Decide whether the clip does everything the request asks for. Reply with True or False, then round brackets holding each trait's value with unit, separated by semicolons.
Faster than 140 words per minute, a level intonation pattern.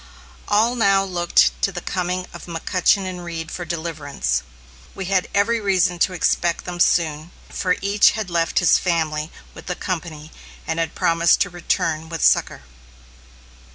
True (155 wpm; 2.3 semitones)